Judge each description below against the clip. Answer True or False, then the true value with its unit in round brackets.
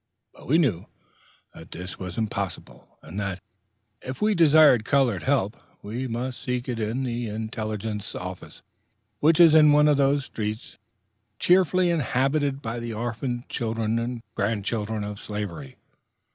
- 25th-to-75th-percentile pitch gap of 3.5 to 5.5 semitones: True (4.7 semitones)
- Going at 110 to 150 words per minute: True (145 wpm)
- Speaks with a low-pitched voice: True (115 Hz)